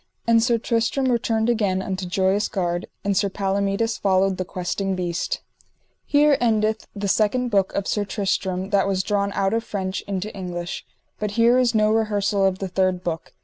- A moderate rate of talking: Yes, average, 180 wpm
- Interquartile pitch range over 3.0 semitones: No, narrow, 2.6 semitones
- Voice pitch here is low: No, high, 200 Hz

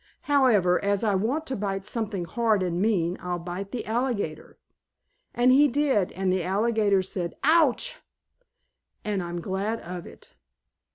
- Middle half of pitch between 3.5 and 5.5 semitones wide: Yes, average, 4.6 semitones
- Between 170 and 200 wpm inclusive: No, average, 150 wpm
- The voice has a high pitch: Yes, high, 200 Hz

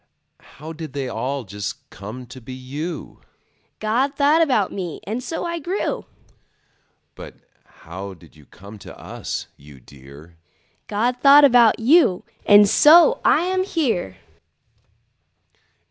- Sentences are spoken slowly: Yes, slow, 130 wpm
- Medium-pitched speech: Yes, medium, 175 Hz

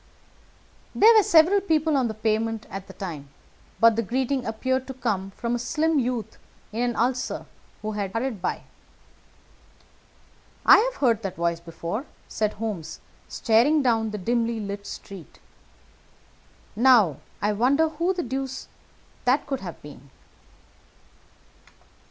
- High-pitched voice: Yes, high, 230 Hz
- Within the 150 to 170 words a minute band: No, slow, 135 wpm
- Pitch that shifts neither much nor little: Yes, average, 4.5 semitones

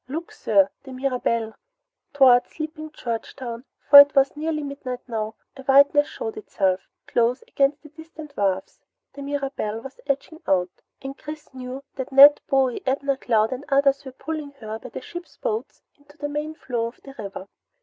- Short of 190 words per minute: Yes, average, 170 wpm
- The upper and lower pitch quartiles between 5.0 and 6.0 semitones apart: No, average, 3.1 semitones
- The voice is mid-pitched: No, very high, 275 Hz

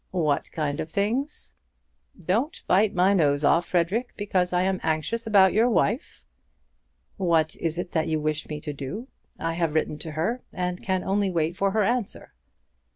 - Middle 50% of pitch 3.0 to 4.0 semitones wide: No, average, 4.4 semitones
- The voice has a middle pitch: Yes, medium, 180 Hz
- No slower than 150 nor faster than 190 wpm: Yes, average, 175 wpm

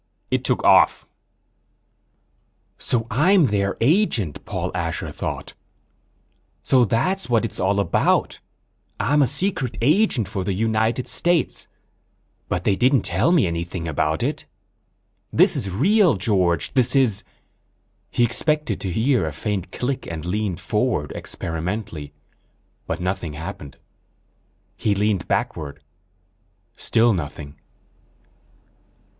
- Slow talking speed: Yes, slow, 115 wpm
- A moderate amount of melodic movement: No, wide, 6.4 semitones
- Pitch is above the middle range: No, low, 105 Hz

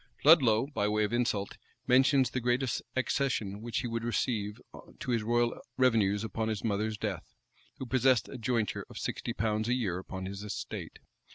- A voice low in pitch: Yes, low, 115 Hz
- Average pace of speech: Yes, average, 175 wpm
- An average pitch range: Yes, average, 3.1 semitones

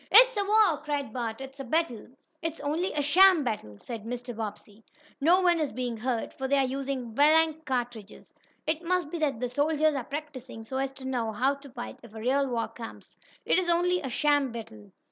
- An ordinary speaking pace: No, fast, 210 wpm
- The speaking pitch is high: Yes, very high, 270 Hz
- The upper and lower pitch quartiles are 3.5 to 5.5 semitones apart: Yes, average, 4.7 semitones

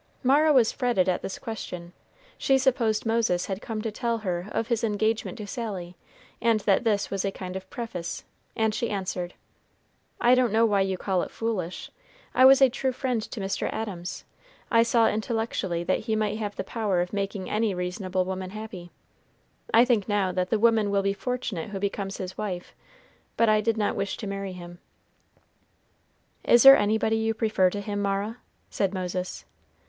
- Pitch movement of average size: Yes, average, 3.2 semitones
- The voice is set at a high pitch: Yes, high, 210 Hz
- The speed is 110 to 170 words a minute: No, average, 185 wpm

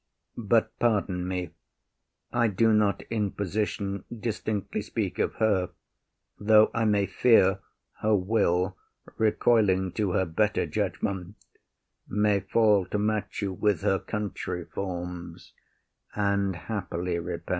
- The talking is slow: Yes, slow, 120 wpm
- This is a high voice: No, low, 100 Hz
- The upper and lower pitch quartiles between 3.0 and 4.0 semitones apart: No, narrow, 2.6 semitones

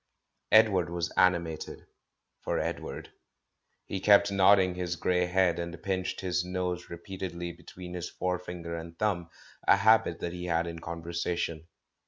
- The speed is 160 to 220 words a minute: No, average, 150 wpm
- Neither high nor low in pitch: No, very low, 90 Hz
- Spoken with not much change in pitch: Yes, narrow, 1.5 semitones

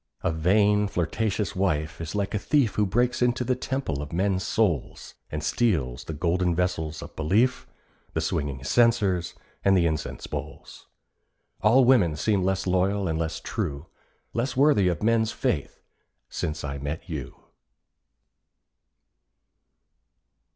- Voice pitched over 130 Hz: No, very low, 95 Hz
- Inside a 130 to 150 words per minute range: Yes, slow, 135 wpm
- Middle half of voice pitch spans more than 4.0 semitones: Yes, wide, 5.5 semitones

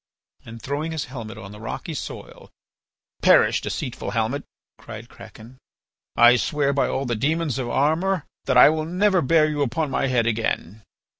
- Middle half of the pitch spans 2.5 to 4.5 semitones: No, average, 4.9 semitones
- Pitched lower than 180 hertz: Yes, low, 135 Hz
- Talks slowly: No, average, 165 wpm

